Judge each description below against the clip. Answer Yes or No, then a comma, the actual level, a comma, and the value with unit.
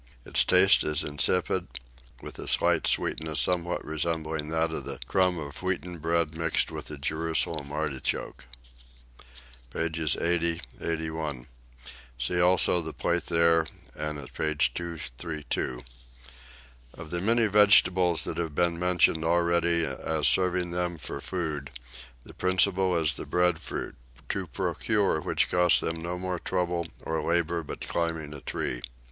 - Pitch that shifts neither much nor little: No, narrow, 2.2 semitones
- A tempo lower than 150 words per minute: Yes, slow, 135 wpm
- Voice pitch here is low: Yes, very low, 85 Hz